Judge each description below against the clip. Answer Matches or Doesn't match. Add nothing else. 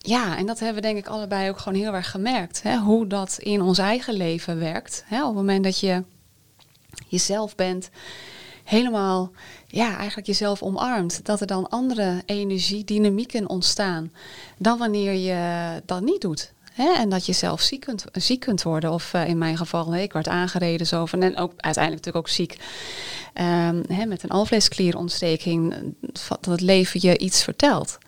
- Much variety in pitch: Doesn't match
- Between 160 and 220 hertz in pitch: Matches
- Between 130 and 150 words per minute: Doesn't match